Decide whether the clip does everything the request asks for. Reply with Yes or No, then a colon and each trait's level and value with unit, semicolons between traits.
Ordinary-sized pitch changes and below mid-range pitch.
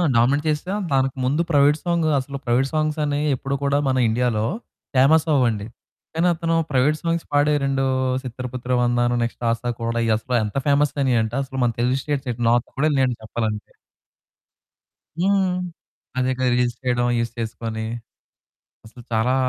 Yes: average, 3.3 semitones; low, 130 Hz